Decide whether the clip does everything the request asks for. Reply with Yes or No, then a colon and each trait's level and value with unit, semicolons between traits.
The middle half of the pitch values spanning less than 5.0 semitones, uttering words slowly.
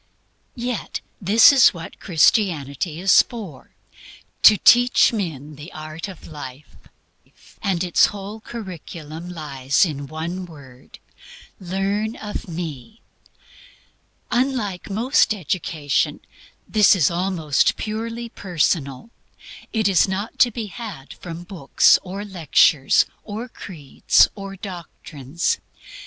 No: average, 5.3 semitones; slow, 110 wpm